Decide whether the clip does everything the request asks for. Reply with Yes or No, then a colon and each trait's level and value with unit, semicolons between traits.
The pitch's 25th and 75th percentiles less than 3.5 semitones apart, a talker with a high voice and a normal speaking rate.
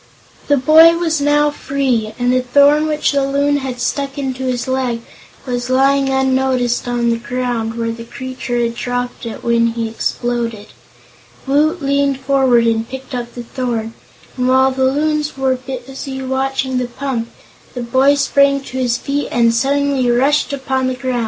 Yes: narrow, 2.4 semitones; very high, 260 Hz; average, 170 wpm